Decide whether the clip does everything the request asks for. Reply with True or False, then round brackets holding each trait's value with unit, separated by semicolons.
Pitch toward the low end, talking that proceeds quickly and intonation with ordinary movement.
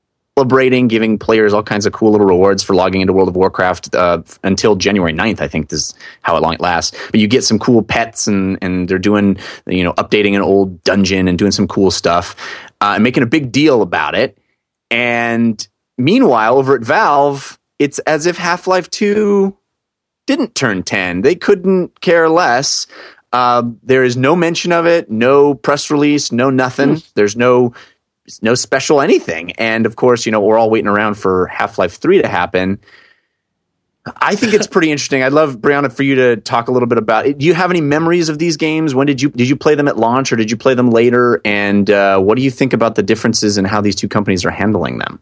False (120 Hz; 215 wpm; 5.9 semitones)